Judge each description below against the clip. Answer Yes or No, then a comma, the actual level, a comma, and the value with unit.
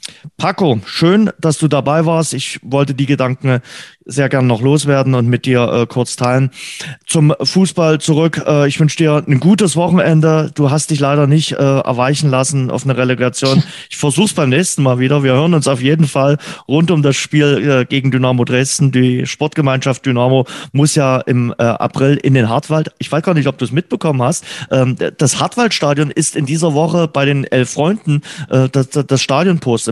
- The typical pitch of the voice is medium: Yes, medium, 145 Hz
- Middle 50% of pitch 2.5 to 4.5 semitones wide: Yes, average, 3.2 semitones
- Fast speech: Yes, fast, 195 wpm